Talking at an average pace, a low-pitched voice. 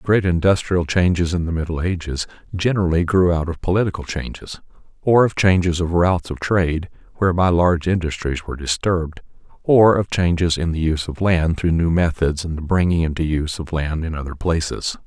Yes: average, 185 wpm; very low, 85 Hz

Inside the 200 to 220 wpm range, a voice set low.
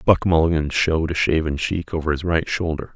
Yes: fast, 205 wpm; very low, 80 Hz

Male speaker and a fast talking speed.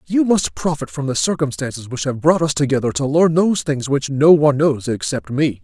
Yes: male; fast, 225 wpm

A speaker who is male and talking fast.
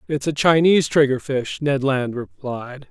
No: male; average, 145 wpm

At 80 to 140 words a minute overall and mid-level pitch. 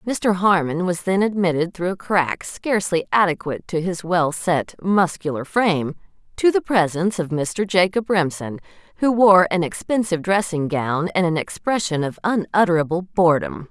No: average, 155 wpm; medium, 175 Hz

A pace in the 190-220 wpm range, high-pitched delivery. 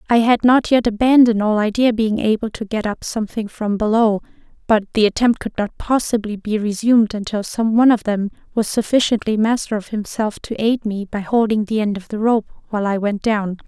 Yes: fast, 205 wpm; high, 220 Hz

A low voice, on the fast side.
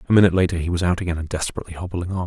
Yes: very low, 90 Hz; fast, 290 wpm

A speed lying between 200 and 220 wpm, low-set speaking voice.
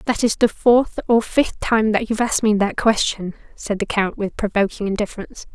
No: fast, 205 wpm; high, 215 Hz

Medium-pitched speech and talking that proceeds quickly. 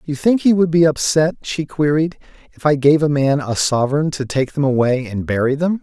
Yes: medium, 150 Hz; fast, 225 wpm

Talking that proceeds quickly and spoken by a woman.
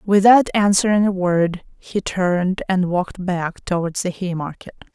No: average, 160 wpm; female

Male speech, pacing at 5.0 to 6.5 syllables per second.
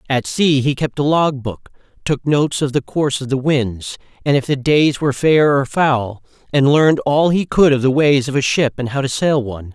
Yes: male; 5.1 syllables/s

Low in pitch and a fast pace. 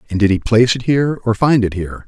Yes: low, 115 Hz; fast, 290 wpm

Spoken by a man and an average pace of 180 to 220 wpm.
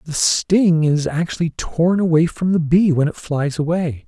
Yes: male; average, 190 wpm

